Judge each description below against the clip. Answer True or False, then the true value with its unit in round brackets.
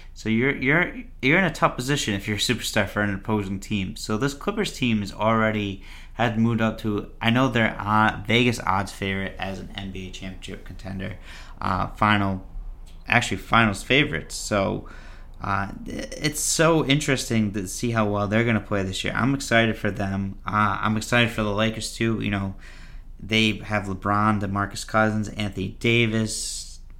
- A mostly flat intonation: False (3.0 semitones)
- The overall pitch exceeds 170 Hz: False (105 Hz)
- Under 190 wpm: True (175 wpm)